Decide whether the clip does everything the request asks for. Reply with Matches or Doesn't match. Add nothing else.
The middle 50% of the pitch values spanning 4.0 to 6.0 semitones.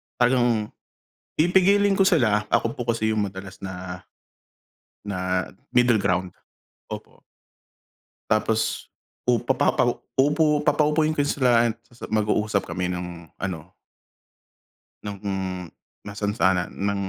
Matches